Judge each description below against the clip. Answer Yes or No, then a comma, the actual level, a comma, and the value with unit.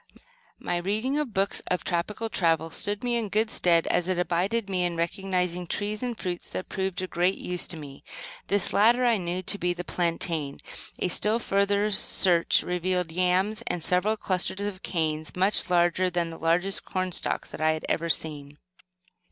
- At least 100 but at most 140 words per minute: No, average, 180 wpm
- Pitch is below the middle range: No, medium, 180 Hz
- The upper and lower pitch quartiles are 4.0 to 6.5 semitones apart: No, average, 3.0 semitones